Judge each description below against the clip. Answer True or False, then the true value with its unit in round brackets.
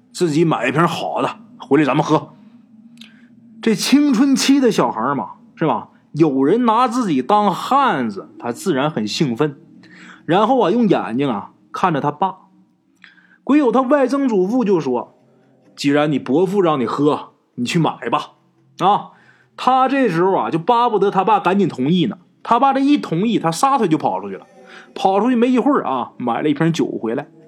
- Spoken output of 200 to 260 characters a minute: True (250 characters per minute)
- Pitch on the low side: False (200 Hz)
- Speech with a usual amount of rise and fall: False (7.3 semitones)